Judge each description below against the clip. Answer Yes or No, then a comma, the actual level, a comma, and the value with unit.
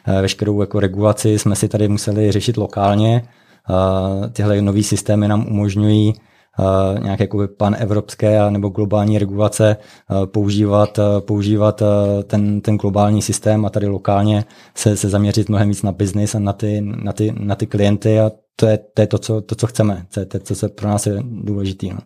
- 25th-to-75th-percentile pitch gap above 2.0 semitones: No, narrow, 0.8 semitones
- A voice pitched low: Yes, low, 105 Hz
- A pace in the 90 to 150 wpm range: No, fast, 170 wpm